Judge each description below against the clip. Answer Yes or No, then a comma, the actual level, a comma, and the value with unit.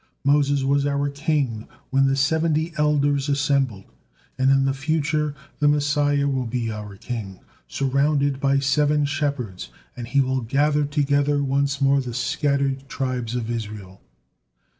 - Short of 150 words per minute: Yes, average, 140 wpm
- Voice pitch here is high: No, medium, 140 Hz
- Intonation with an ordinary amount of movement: No, narrow, 2.0 semitones